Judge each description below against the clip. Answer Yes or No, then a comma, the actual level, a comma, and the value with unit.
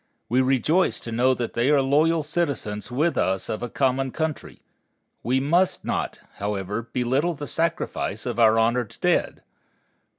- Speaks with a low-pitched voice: Yes, low, 130 Hz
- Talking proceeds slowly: No, average, 155 wpm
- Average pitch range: Yes, average, 4.4 semitones